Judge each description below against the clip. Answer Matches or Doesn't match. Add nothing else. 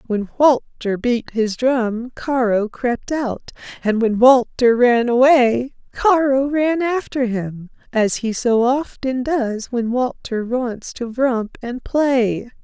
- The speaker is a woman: Matches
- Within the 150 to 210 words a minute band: Doesn't match